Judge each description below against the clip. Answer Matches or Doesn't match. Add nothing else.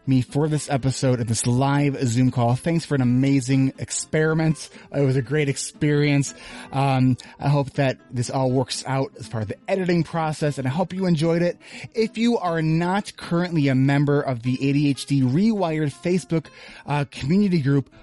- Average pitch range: Matches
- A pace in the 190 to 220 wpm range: Doesn't match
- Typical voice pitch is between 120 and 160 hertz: Matches